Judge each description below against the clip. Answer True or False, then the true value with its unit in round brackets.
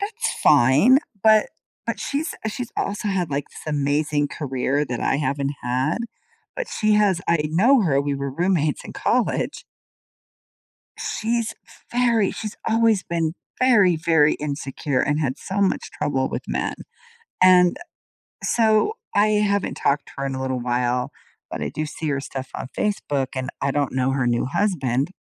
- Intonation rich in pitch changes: True (7.2 semitones)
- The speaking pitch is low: False (155 Hz)